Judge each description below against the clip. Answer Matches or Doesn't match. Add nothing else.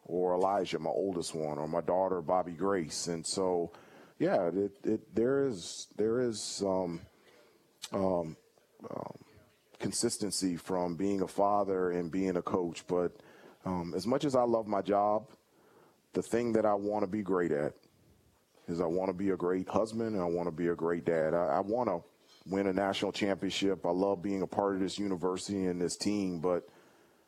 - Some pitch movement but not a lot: Doesn't match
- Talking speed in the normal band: Matches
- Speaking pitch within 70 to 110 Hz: Matches